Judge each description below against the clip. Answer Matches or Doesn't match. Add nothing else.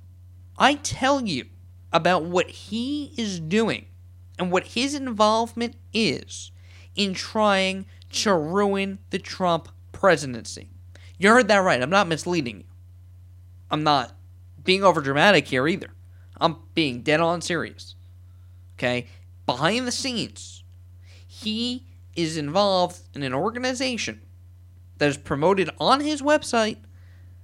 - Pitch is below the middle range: Doesn't match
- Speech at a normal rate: Doesn't match